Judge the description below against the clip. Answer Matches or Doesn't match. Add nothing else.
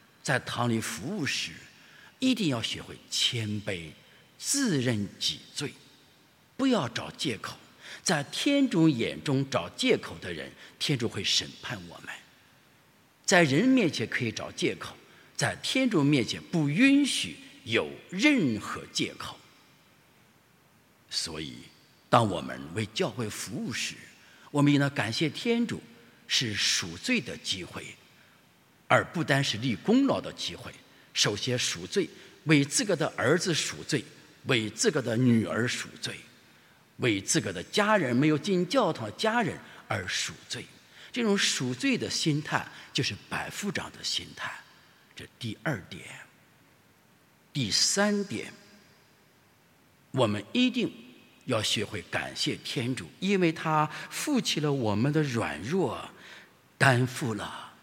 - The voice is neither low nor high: Matches